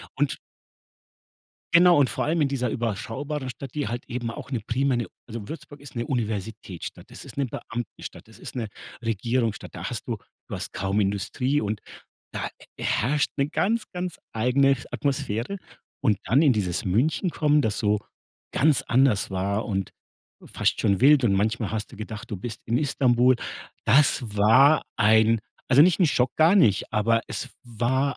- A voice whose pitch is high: No, low, 120 Hz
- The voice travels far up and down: No, average, 4.5 semitones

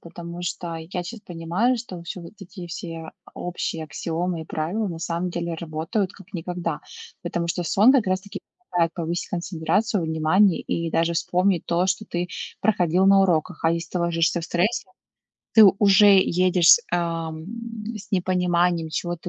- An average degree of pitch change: No, narrow, 2.0 semitones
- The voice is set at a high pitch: No, medium, 175 Hz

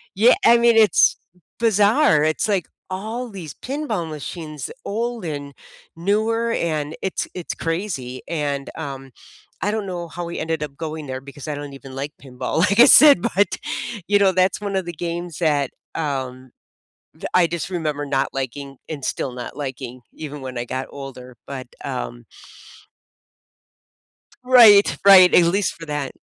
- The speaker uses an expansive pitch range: Yes, wide, 6.2 semitones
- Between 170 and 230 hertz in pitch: No, medium, 160 Hz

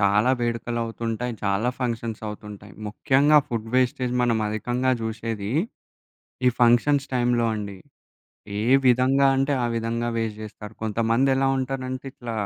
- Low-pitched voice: Yes, low, 115 Hz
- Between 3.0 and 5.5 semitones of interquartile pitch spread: No, narrow, 2.5 semitones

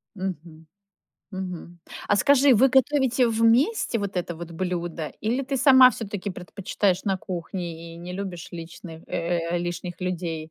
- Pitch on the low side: No, medium, 185 Hz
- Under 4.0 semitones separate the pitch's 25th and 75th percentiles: No, average, 5.0 semitones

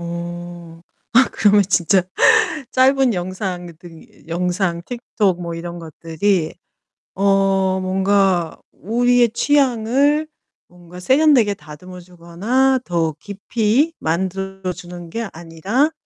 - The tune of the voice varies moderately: Yes, average, 4.8 semitones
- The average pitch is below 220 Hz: Yes, high, 190 Hz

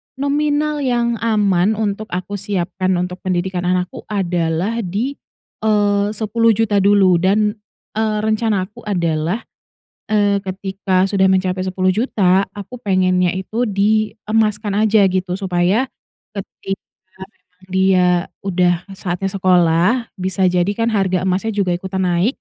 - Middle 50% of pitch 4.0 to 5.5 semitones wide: No, average, 2.8 semitones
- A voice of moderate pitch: No, high, 195 Hz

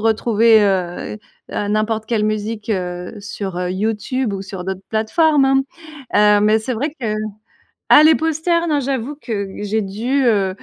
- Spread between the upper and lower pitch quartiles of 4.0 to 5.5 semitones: Yes, average, 4.3 semitones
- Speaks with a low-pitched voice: No, high, 220 Hz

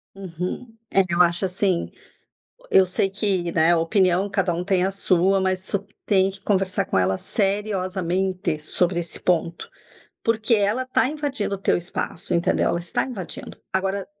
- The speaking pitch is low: No, high, 190 Hz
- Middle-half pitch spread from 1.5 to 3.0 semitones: Yes, narrow, 2.4 semitones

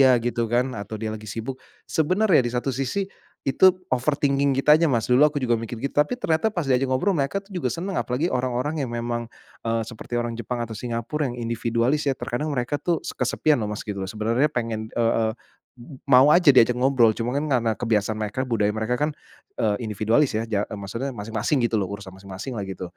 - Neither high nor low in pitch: No, low, 120 Hz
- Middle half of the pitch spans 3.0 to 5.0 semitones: Yes, average, 3.9 semitones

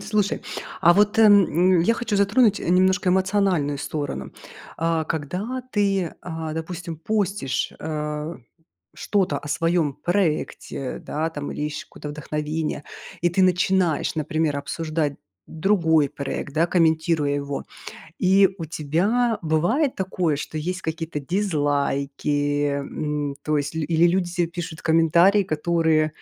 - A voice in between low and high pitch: Yes, medium, 165 Hz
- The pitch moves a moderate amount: Yes, average, 3.8 semitones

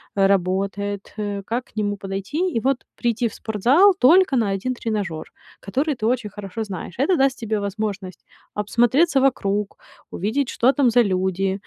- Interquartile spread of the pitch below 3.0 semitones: No, average, 4.5 semitones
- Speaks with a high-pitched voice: Yes, high, 215 Hz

